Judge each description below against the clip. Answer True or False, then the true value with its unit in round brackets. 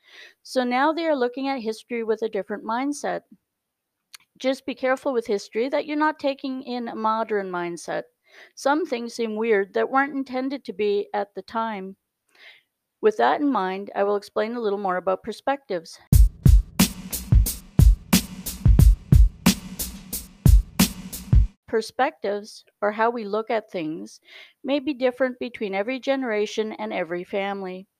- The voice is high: True (225 Hz)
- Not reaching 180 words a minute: True (135 wpm)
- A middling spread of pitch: True (4.8 semitones)